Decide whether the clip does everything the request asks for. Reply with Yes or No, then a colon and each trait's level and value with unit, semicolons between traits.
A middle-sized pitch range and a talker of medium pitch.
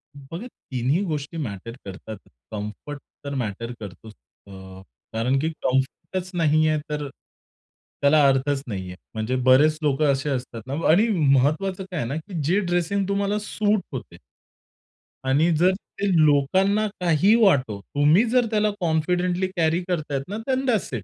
No: wide, 5.7 semitones; medium, 150 Hz